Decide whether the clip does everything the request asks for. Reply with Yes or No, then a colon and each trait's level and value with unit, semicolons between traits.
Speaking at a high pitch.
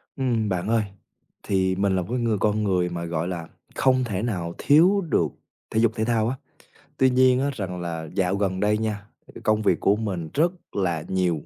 No: low, 105 Hz